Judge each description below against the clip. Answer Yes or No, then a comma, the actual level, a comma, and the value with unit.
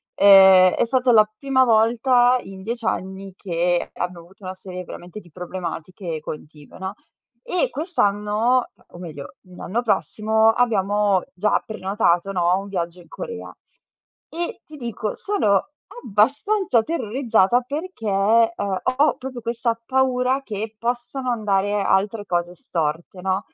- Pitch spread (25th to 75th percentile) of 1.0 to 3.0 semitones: No, average, 4.6 semitones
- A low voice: No, high, 210 Hz